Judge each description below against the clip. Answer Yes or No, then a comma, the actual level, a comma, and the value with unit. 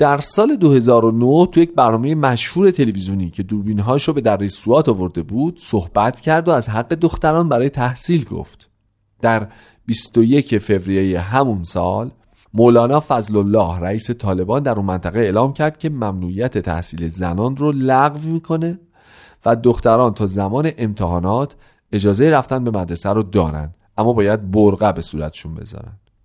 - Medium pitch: No, low, 115 Hz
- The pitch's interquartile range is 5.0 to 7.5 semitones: Yes, average, 5.3 semitones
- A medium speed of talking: Yes, average, 145 wpm